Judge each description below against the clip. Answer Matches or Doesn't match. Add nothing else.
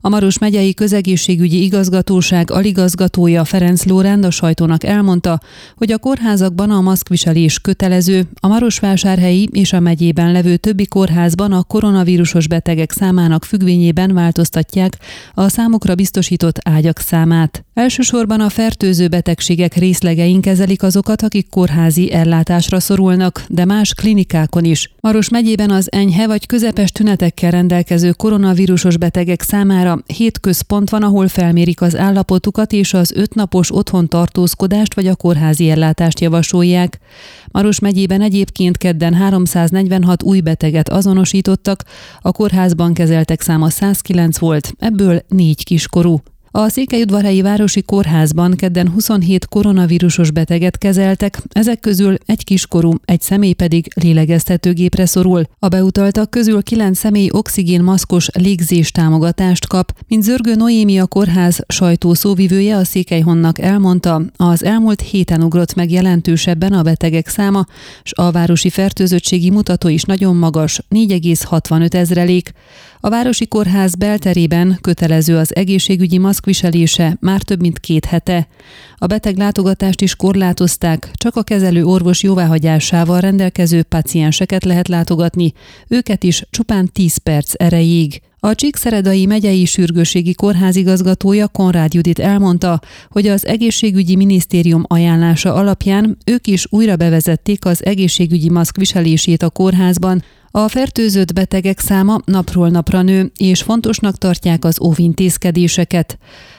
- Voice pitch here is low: Doesn't match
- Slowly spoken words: Doesn't match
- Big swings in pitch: Doesn't match